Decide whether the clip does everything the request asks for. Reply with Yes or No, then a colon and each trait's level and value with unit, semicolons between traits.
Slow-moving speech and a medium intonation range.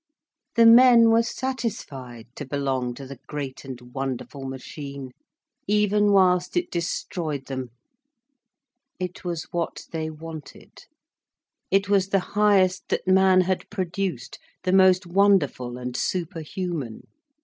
No: slow, 120 wpm; wide, 6.1 semitones